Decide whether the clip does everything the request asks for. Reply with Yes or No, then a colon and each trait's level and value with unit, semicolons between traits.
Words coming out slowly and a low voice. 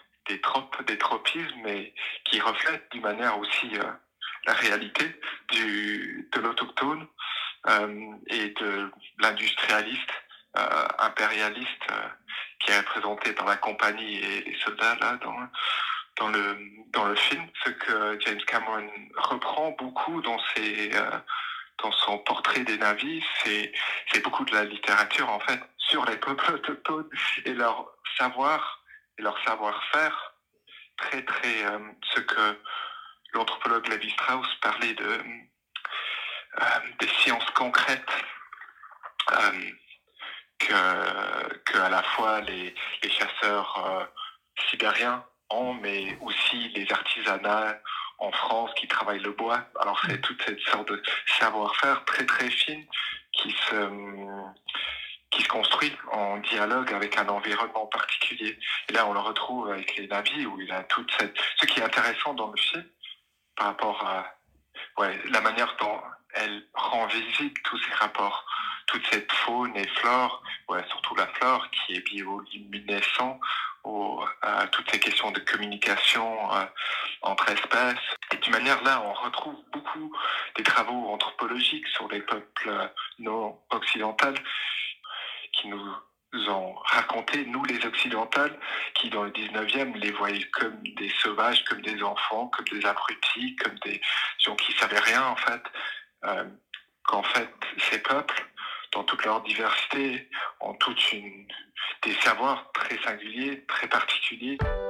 Yes: slow, 140 wpm; low, 110 Hz